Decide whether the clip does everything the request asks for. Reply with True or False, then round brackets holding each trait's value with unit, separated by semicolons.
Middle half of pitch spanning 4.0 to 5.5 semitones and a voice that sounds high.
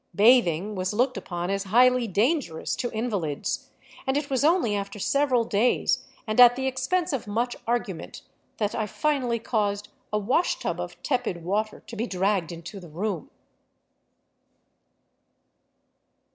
True (4.3 semitones; 220 Hz)